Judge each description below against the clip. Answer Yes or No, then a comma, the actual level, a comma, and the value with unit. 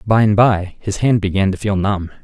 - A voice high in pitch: No, low, 100 Hz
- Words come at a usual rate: No, fast, 240 wpm